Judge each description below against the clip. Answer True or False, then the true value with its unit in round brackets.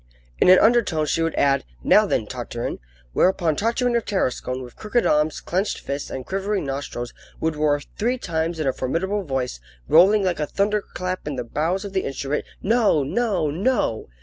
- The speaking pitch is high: False (170 Hz)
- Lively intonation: True (5.9 semitones)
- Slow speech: False (175 wpm)